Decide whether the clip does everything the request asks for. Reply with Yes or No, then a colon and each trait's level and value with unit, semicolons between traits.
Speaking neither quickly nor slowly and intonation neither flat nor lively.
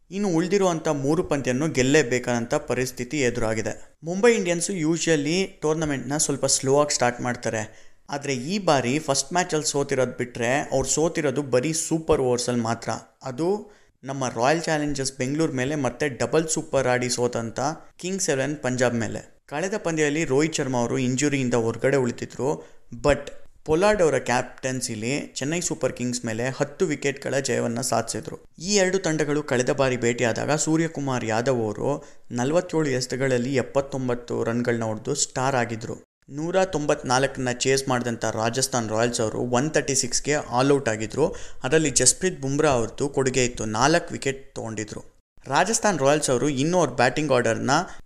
No: fast, 135 wpm; average, 4.0 semitones